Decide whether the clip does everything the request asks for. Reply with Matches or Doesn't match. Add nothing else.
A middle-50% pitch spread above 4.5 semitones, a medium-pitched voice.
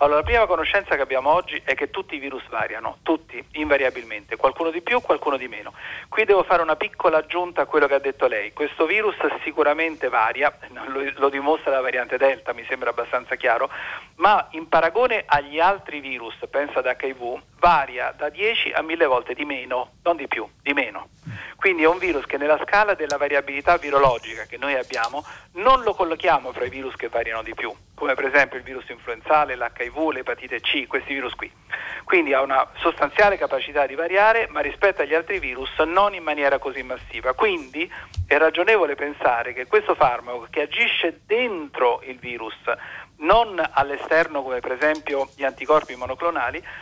Matches